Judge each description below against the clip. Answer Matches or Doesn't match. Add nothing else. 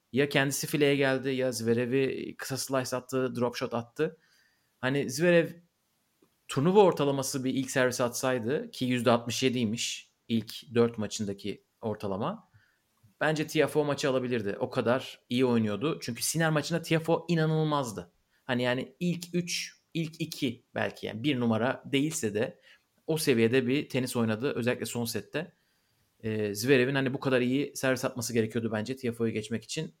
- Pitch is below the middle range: Matches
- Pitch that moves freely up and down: Doesn't match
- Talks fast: Matches